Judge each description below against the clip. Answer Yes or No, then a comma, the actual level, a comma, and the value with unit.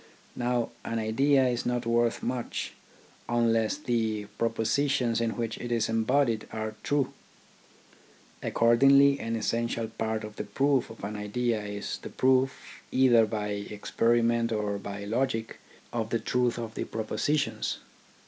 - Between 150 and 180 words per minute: No, average, 140 wpm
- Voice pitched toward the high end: No, low, 115 Hz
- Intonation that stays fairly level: Yes, narrow, 2.0 semitones